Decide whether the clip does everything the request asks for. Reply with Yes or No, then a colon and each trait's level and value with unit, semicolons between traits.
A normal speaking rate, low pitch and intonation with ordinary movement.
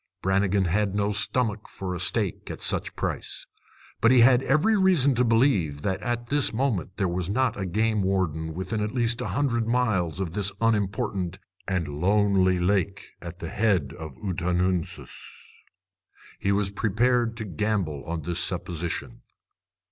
Yes: average, 160 wpm; low, 100 Hz; average, 4.2 semitones